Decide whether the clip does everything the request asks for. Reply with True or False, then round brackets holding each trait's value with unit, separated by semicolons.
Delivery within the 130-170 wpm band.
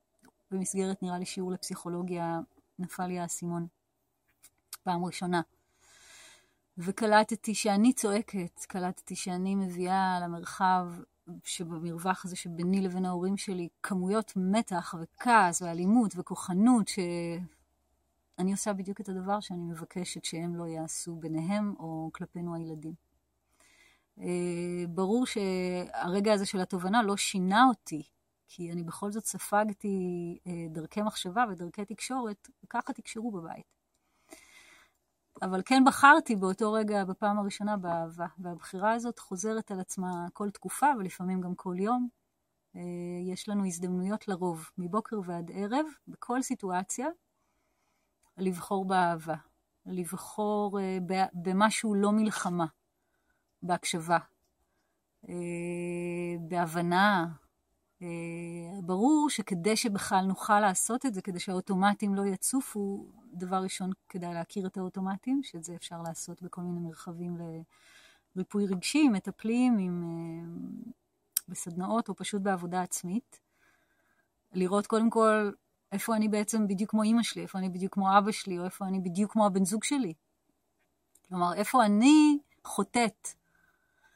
False (115 wpm)